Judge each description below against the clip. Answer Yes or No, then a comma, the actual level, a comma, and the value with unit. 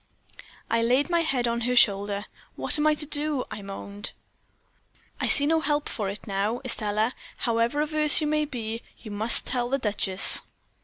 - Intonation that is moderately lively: No, wide, 5.9 semitones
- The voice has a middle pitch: No, high, 240 Hz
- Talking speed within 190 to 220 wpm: No, average, 175 wpm